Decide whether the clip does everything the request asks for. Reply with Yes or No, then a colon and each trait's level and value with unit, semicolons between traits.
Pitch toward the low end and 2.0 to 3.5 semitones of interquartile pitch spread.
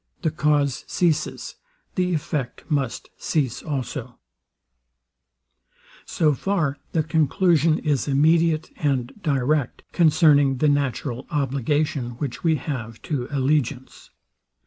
No: medium, 145 Hz; average, 2.7 semitones